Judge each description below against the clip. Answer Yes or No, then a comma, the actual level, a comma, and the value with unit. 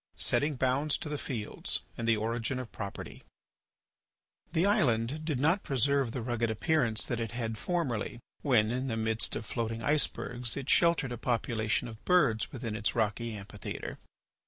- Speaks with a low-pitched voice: Yes, low, 120 Hz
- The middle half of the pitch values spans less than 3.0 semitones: No, average, 3.9 semitones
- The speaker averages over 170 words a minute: No, average, 165 wpm